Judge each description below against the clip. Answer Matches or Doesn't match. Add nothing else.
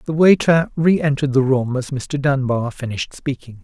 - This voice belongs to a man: Matches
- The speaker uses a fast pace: Doesn't match